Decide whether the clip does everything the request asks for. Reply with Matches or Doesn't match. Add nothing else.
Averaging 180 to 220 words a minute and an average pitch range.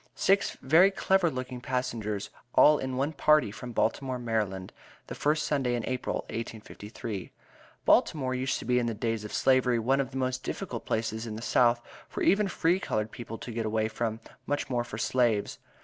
Matches